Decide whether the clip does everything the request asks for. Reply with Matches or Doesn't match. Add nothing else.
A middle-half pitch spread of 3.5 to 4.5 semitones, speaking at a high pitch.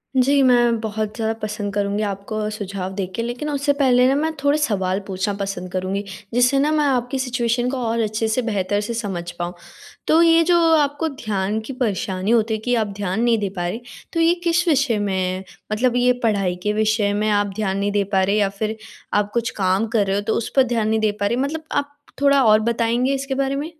Matches